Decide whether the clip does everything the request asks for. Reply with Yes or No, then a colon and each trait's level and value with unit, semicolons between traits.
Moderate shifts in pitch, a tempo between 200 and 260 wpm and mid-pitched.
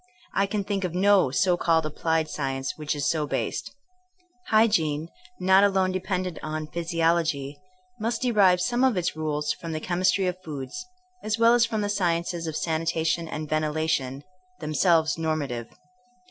No: average, 3.7 semitones; average, 160 wpm; medium, 165 Hz